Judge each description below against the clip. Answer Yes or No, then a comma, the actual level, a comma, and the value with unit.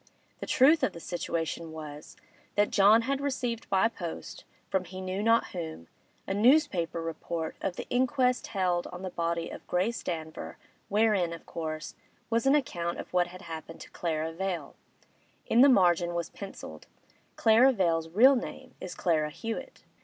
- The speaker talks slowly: No, average, 165 wpm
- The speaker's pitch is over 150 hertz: Yes, medium, 185 Hz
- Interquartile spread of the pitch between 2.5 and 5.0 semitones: No, wide, 5.4 semitones